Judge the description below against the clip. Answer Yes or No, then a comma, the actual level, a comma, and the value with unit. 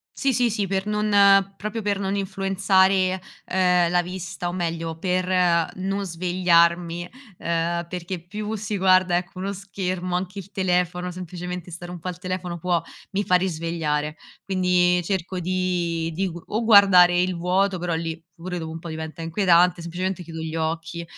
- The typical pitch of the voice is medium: Yes, medium, 180 Hz